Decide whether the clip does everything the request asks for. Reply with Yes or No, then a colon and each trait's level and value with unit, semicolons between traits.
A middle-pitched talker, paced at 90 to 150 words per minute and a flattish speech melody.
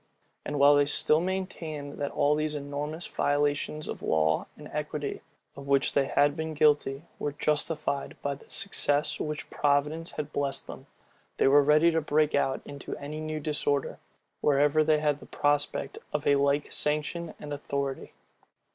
No: medium, 145 Hz; average, 165 wpm; narrow, 1.3 semitones